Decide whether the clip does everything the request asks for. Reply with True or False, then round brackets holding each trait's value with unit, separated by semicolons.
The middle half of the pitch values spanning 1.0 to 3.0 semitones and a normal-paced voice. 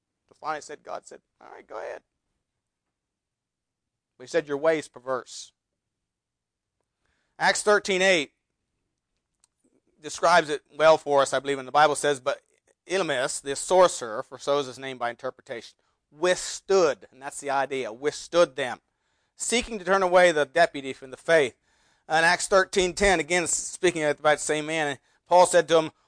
False (4.5 semitones; 155 wpm)